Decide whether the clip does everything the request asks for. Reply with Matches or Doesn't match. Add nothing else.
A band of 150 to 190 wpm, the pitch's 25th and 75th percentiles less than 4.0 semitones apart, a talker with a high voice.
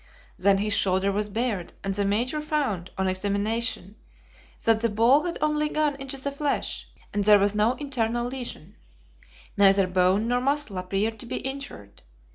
Doesn't match